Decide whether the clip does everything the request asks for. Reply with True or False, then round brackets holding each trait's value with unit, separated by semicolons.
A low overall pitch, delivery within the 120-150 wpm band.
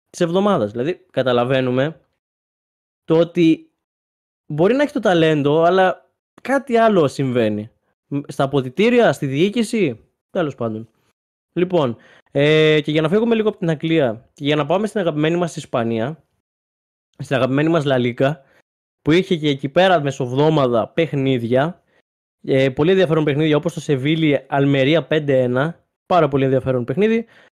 False (155 Hz; 135 wpm)